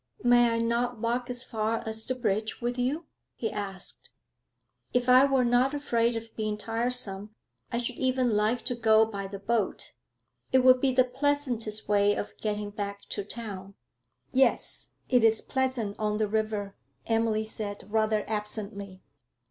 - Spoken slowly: No, average, 160 wpm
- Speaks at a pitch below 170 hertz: No, high, 225 Hz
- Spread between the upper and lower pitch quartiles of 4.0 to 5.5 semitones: No, average, 2.8 semitones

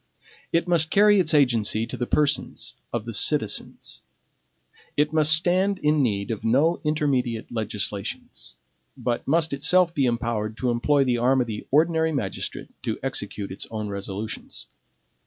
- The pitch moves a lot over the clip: Yes, wide, 6.0 semitones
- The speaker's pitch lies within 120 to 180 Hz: Yes, low, 135 Hz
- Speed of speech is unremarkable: Yes, average, 150 wpm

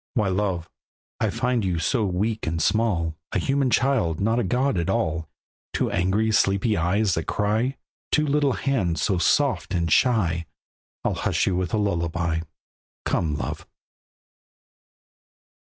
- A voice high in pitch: No, low, 100 Hz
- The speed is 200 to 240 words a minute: No, average, 145 wpm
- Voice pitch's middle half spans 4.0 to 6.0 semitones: Yes, wide, 5.5 semitones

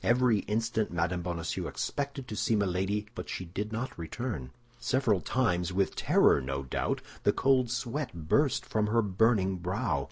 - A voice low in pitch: Yes, low, 105 Hz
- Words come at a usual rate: Yes, average, 160 wpm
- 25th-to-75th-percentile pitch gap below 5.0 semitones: No, average, 5.3 semitones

